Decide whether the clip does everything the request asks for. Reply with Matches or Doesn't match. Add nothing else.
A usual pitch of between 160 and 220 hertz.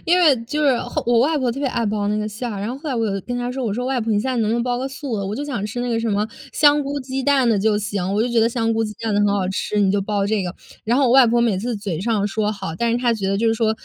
Doesn't match